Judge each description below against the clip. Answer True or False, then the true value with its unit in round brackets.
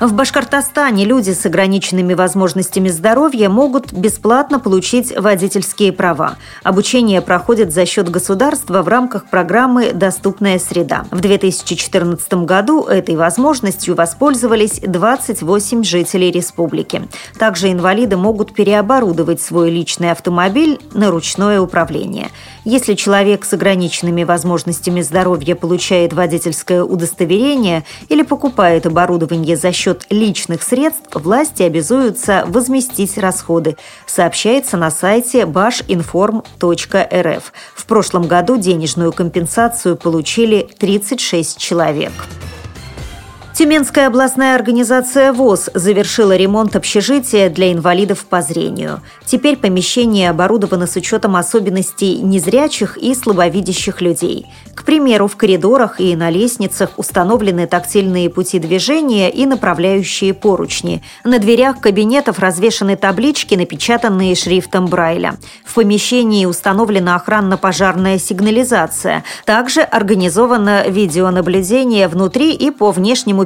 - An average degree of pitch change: True (4.4 semitones)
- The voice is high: True (195 Hz)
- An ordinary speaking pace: False (105 wpm)